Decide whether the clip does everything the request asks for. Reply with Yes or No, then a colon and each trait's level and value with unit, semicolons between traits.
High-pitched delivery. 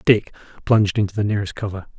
No: low, 105 Hz